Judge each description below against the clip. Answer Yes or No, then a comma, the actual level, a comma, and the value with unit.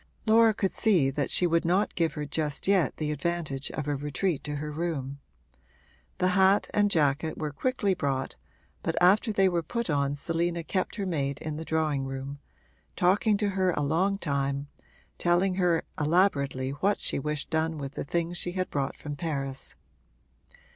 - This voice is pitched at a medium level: Yes, medium, 160 Hz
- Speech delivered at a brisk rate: No, average, 175 wpm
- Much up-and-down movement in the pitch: No, average, 4.5 semitones